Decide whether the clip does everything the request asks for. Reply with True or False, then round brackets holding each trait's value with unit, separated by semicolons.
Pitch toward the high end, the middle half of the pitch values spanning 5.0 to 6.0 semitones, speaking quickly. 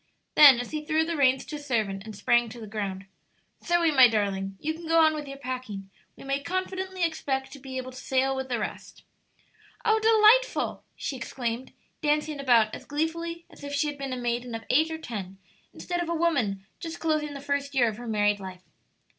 True (270 Hz; 5.4 semitones; 215 wpm)